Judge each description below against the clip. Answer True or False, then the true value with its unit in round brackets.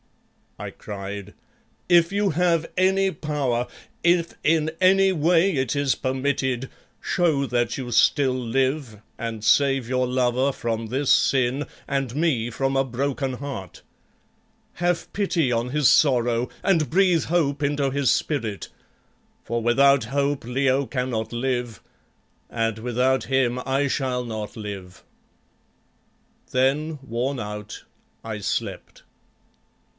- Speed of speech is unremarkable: False (120 wpm)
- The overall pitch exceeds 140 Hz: False (130 Hz)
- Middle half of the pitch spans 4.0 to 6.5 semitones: False (3.6 semitones)